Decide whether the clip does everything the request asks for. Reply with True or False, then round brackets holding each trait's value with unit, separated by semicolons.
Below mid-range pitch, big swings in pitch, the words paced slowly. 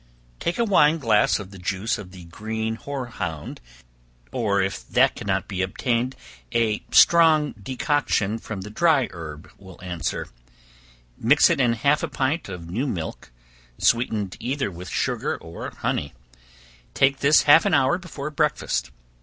False (115 Hz; 7.1 semitones; 150 wpm)